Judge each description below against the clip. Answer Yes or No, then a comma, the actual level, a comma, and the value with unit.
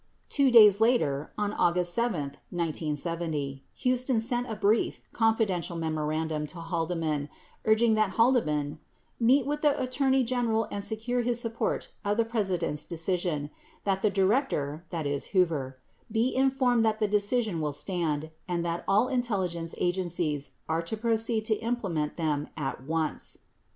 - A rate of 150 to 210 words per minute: No, average, 140 wpm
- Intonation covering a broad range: Yes, wide, 6.2 semitones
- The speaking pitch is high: Yes, high, 195 Hz